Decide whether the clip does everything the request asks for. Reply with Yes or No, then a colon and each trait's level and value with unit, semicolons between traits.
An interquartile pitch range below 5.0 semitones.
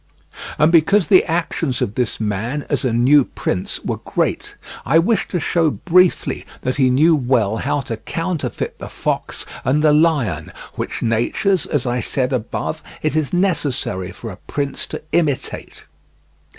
No: wide, 5.4 semitones